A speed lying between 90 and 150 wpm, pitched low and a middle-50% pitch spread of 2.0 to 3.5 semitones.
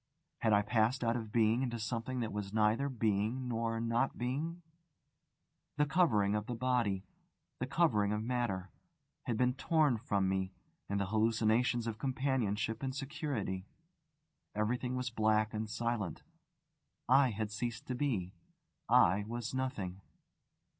Yes: average, 140 wpm; low, 115 Hz; average, 3.1 semitones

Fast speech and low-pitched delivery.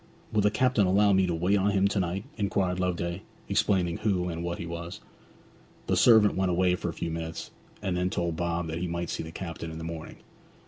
Yes: fast, 225 wpm; very low, 90 Hz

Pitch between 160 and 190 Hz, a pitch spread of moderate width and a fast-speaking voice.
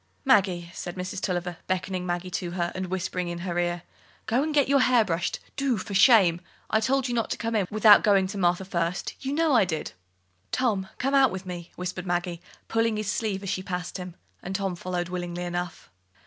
Yes: medium, 185 Hz; average, 3.7 semitones; fast, 210 wpm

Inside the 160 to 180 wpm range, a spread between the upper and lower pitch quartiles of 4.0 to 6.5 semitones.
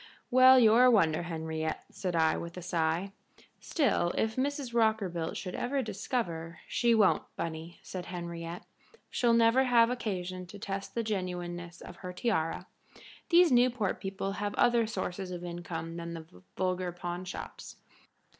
No: average, 150 wpm; average, 5.2 semitones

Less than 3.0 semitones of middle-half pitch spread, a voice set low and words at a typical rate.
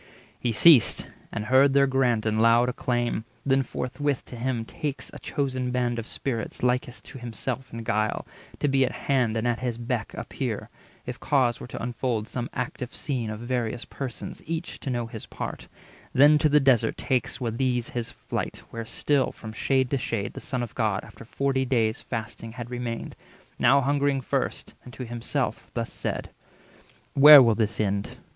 Yes: narrow, 2.6 semitones; low, 125 Hz; average, 185 wpm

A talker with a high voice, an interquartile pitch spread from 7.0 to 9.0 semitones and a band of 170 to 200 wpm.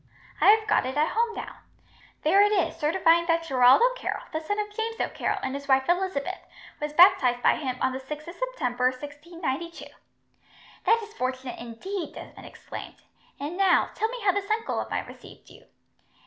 Yes: very high, 335 Hz; wide, 7.5 semitones; average, 185 wpm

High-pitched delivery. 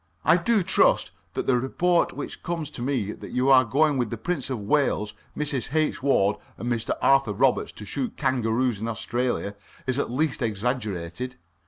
No: low, 125 Hz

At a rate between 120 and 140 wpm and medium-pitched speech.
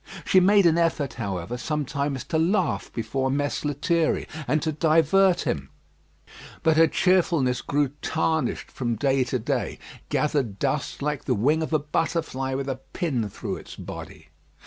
No: average, 155 wpm; medium, 145 Hz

